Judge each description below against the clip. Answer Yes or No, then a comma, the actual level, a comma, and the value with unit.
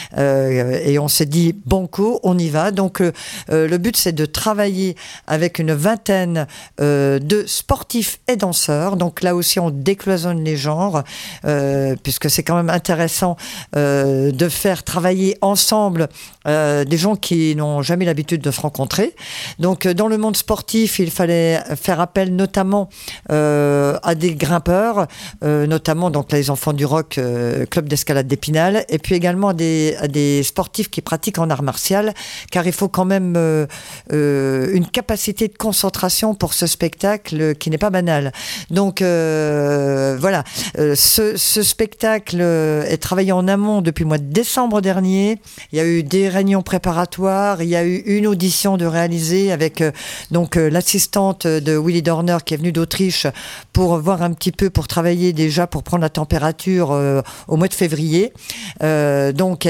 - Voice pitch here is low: No, medium, 175 Hz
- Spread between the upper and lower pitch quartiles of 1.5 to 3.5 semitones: No, average, 4.0 semitones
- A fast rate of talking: No, average, 175 wpm